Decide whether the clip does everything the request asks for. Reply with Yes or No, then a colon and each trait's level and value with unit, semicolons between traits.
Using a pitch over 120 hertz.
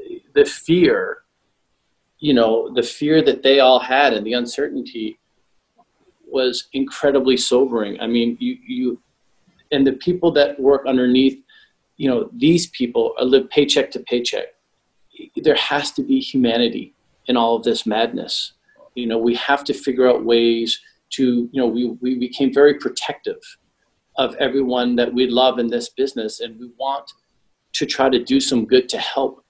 Yes: low, 135 Hz